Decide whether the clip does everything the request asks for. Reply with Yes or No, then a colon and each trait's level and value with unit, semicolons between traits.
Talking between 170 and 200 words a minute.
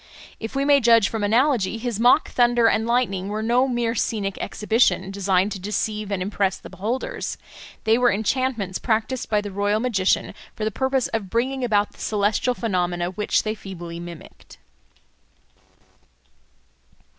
No: average, 155 wpm